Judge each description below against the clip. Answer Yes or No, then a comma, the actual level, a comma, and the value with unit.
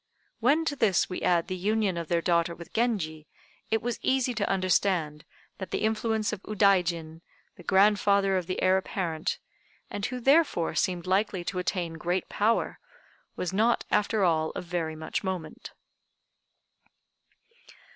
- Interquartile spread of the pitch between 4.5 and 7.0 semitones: No, average, 3.9 semitones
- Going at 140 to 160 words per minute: Yes, average, 150 wpm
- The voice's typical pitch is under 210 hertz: Yes, high, 190 Hz